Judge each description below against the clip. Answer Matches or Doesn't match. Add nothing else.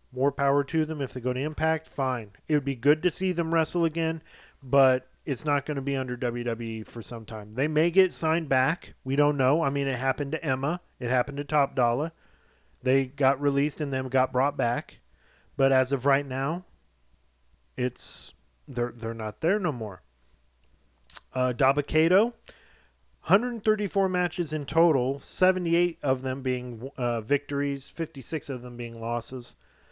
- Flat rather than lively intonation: Doesn't match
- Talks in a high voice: Doesn't match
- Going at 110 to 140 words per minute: Doesn't match